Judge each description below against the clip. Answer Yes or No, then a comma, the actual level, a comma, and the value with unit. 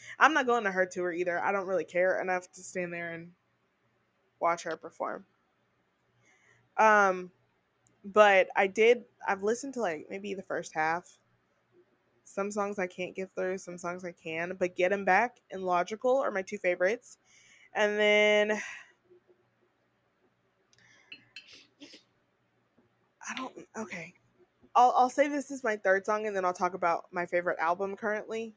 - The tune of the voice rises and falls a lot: No, average, 3.3 semitones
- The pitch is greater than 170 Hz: Yes, high, 190 Hz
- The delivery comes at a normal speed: Yes, average, 155 wpm